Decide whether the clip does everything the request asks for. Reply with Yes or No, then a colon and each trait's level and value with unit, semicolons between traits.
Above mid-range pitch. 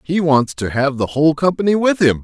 No: medium, 150 Hz